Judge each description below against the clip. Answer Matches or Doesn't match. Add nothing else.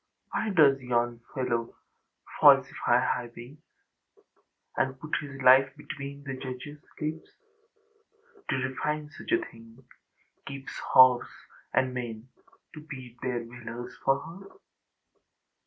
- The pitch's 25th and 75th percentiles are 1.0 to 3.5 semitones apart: Matches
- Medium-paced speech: Doesn't match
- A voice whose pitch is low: Matches